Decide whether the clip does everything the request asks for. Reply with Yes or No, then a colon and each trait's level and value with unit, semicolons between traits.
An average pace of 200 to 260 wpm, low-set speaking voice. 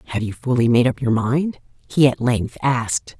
Yes: fast, 205 wpm; low, 125 Hz